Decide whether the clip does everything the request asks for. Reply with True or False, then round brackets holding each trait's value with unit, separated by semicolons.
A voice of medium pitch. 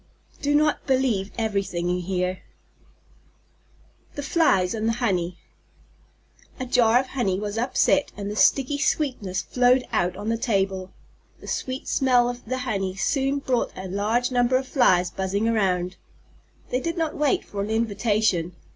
False (225 Hz)